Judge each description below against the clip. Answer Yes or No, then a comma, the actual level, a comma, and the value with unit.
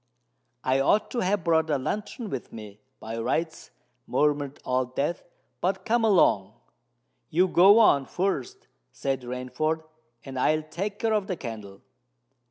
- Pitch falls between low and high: Yes, medium, 155 Hz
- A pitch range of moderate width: No, wide, 6.9 semitones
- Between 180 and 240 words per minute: No, average, 145 wpm